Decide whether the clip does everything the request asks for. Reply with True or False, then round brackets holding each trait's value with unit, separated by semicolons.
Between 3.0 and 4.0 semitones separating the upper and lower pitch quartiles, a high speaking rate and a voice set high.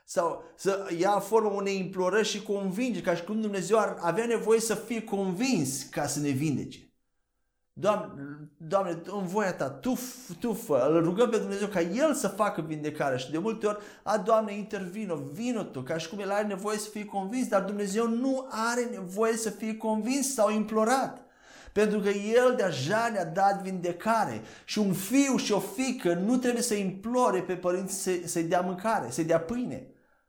True (3.6 semitones; 180 wpm; 205 Hz)